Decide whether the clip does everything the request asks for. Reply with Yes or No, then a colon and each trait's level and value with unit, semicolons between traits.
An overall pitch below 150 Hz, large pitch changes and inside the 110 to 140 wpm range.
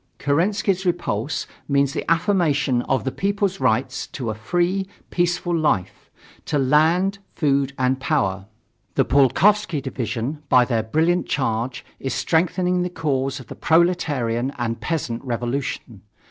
Yes: medium, 140 Hz; wide, 5.7 semitones; slow, 135 wpm